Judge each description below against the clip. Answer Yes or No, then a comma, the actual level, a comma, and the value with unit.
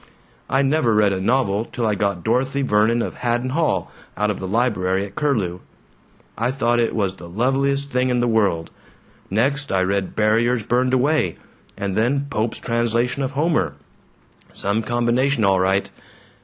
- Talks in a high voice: No, low, 115 Hz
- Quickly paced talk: No, average, 165 wpm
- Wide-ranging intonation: No, average, 4.4 semitones